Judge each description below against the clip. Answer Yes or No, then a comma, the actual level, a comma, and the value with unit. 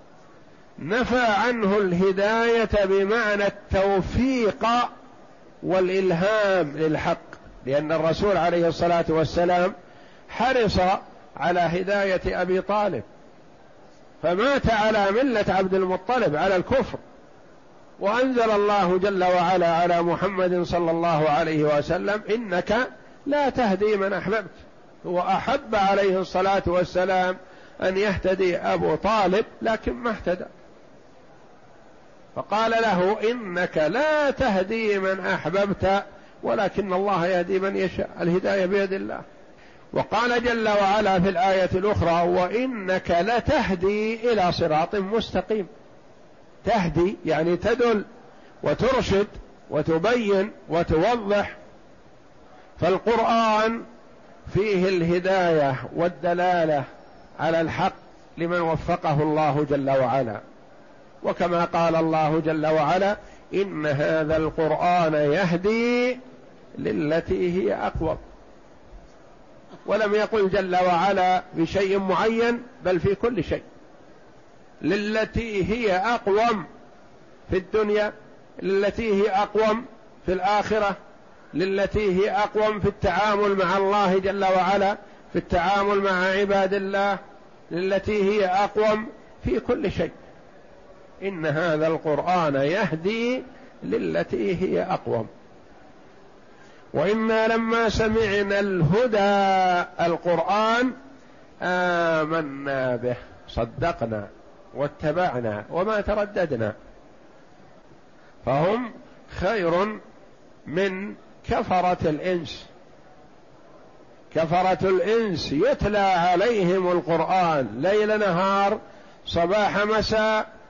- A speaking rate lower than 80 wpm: No, average, 90 wpm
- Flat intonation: No, average, 3.3 semitones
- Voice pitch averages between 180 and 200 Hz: Yes, high, 190 Hz